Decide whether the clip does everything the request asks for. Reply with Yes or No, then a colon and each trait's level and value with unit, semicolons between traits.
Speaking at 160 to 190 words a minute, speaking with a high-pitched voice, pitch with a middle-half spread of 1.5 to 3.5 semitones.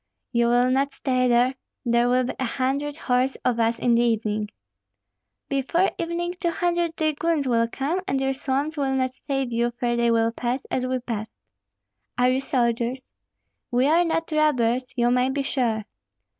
Yes: average, 175 wpm; very high, 255 Hz; average, 2.8 semitones